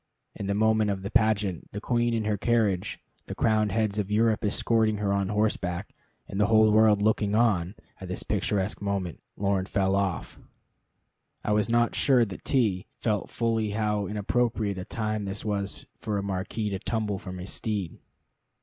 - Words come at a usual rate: Yes, average, 175 wpm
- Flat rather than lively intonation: Yes, narrow, 1.8 semitones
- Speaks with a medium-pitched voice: No, low, 105 Hz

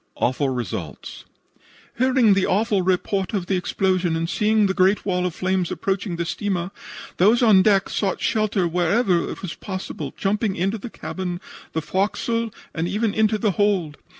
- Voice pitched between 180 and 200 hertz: Yes, high, 190 Hz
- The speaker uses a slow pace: No, average, 165 wpm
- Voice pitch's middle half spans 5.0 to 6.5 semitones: No, average, 3.0 semitones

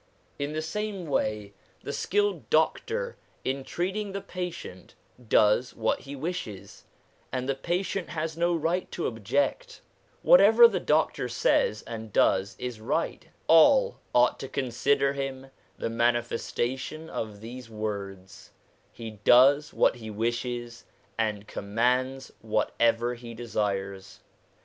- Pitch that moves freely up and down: Yes, wide, 6.4 semitones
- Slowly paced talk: Yes, slow, 130 wpm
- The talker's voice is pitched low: Yes, low, 125 Hz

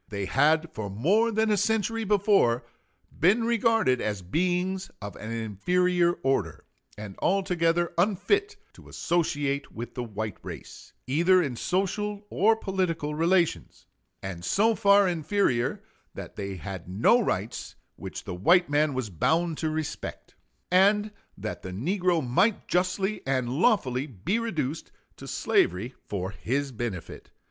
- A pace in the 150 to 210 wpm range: No, slow, 135 wpm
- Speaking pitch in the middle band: Yes, medium, 165 Hz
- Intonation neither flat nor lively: No, wide, 8.6 semitones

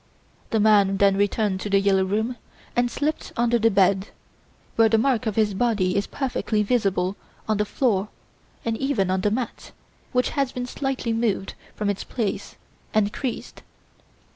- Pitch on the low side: No, high, 215 Hz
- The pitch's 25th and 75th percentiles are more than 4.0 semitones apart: No, average, 3.3 semitones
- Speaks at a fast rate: No, average, 165 wpm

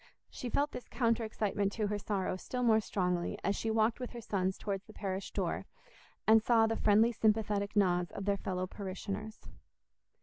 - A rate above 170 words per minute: Yes, average, 180 wpm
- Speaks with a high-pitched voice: Yes, high, 210 Hz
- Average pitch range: No, narrow, 2.3 semitones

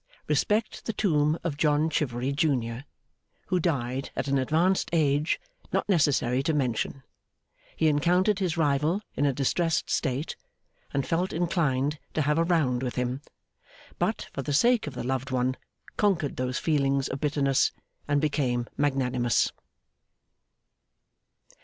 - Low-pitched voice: No, medium, 145 Hz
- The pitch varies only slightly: No, average, 3.7 semitones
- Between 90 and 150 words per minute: Yes, average, 140 wpm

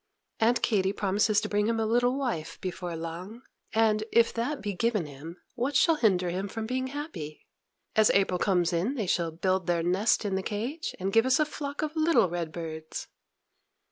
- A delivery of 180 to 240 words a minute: Yes, average, 195 wpm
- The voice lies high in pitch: Yes, high, 210 Hz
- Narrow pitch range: No, average, 5.1 semitones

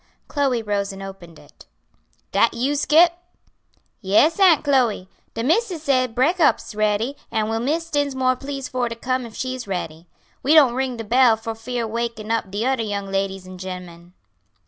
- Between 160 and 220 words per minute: Yes, average, 170 wpm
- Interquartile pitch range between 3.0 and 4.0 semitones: No, average, 4.9 semitones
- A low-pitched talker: No, high, 235 Hz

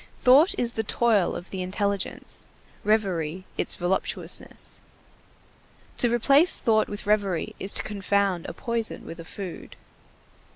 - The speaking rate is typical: No, slow, 130 wpm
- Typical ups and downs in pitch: Yes, average, 3.6 semitones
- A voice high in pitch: Yes, high, 205 Hz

